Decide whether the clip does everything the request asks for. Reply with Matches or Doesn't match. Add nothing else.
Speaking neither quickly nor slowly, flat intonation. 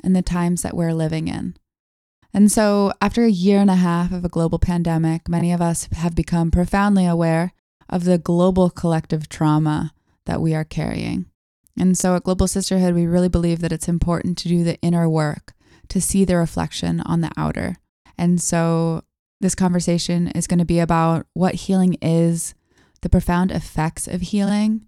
Matches